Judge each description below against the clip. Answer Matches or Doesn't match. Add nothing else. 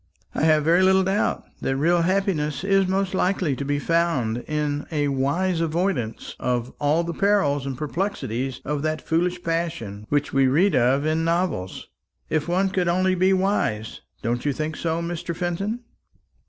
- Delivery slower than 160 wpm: Doesn't match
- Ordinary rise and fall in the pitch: Matches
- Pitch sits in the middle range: Matches